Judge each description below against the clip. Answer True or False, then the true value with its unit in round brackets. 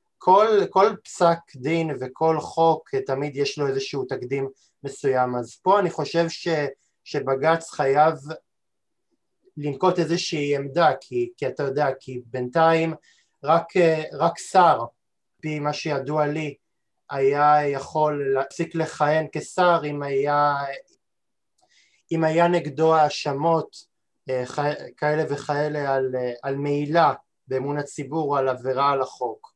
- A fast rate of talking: False (115 wpm)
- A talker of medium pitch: True (150 Hz)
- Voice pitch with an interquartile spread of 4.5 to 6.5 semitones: False (3.0 semitones)